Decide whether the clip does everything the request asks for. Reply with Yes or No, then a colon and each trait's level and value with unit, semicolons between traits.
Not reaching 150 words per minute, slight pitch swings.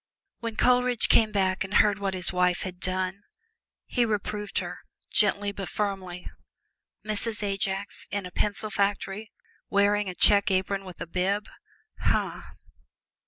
Yes: average, 140 wpm; narrow, 1.9 semitones